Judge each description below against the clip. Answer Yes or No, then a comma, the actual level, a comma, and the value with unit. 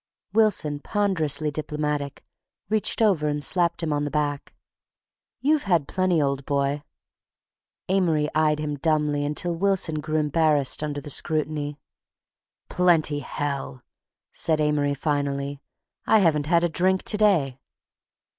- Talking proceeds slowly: Yes, slow, 125 wpm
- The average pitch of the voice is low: No, medium, 150 Hz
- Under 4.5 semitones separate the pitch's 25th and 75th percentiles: Yes, average, 3.0 semitones